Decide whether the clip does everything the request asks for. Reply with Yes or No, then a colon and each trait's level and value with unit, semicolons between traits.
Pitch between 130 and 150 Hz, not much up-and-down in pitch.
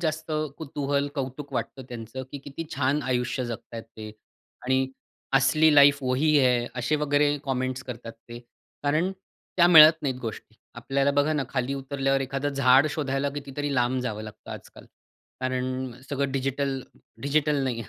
Yes: low, 135 Hz; narrow, 2.1 semitones